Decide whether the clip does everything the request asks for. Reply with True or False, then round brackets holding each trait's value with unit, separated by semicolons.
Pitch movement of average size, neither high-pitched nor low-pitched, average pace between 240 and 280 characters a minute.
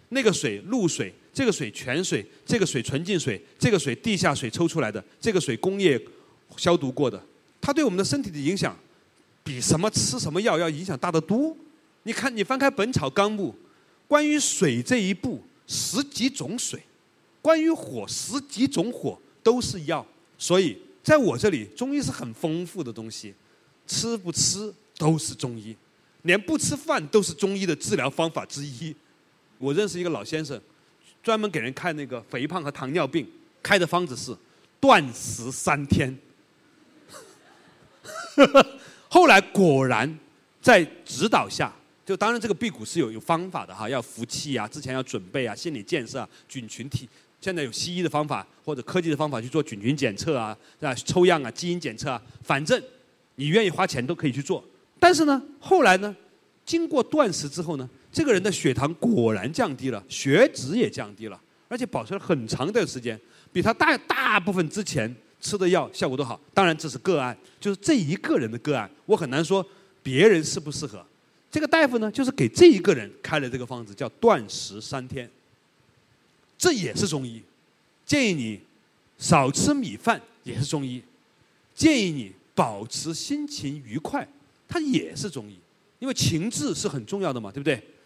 False (7.8 semitones; 165 Hz; 260 characters per minute)